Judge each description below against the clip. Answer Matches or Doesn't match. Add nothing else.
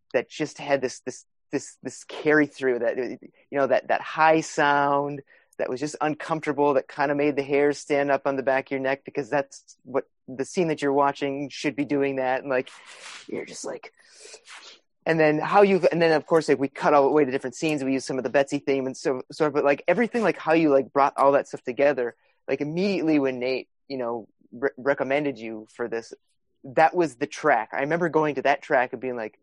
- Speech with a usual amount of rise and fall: Doesn't match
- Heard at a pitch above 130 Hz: Matches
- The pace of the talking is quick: Matches